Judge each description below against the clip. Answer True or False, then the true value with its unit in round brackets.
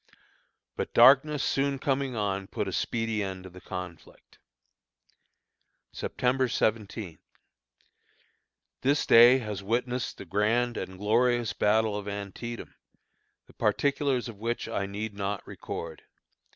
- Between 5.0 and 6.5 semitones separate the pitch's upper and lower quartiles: False (3.9 semitones)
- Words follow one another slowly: True (120 wpm)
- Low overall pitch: True (110 Hz)